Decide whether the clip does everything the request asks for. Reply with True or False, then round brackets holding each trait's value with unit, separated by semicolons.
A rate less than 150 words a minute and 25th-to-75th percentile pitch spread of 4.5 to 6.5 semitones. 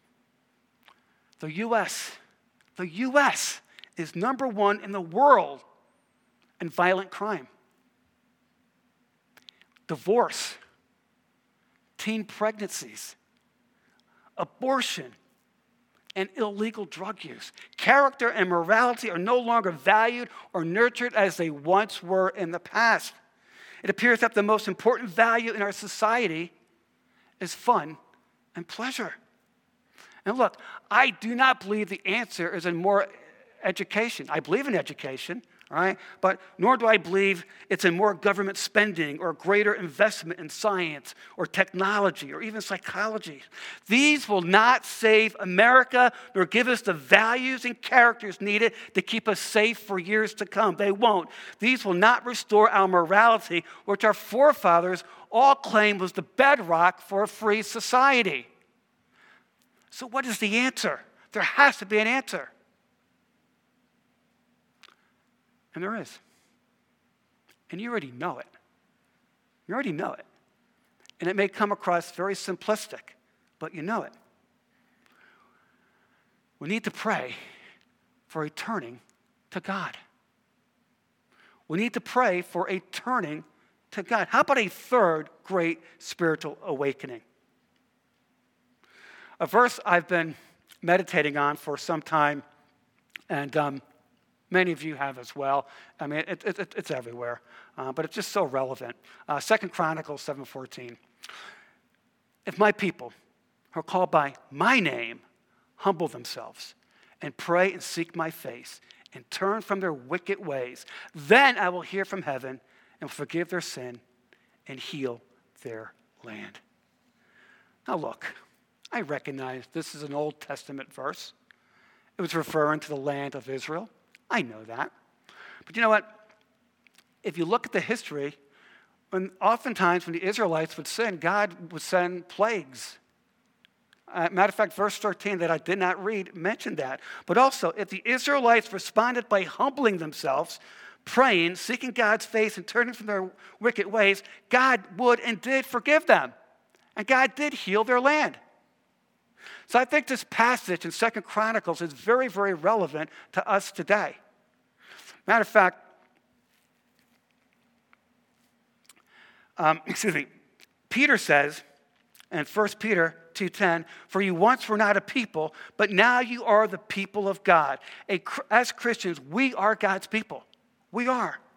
True (140 wpm; 5.1 semitones)